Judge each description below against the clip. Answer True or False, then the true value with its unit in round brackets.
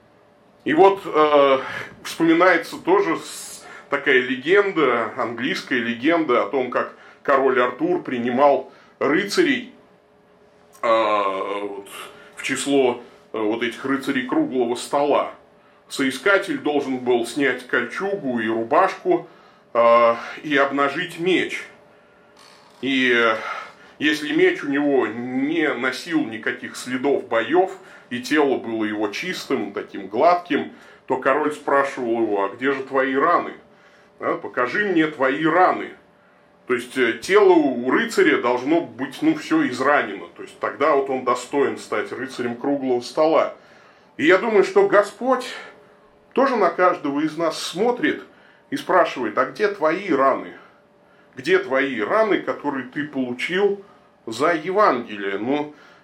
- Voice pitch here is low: False (145 Hz)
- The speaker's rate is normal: True (125 wpm)